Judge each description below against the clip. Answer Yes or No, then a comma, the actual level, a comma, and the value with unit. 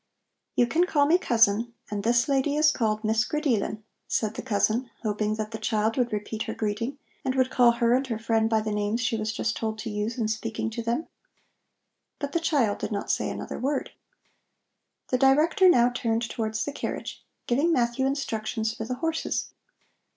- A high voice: Yes, high, 230 Hz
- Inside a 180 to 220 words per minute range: Yes, average, 190 wpm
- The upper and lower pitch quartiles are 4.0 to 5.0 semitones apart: No, average, 3.4 semitones